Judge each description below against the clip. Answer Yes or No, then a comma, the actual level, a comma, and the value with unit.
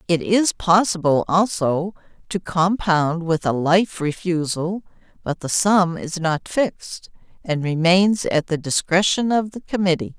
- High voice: No, medium, 175 Hz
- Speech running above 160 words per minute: No, average, 140 wpm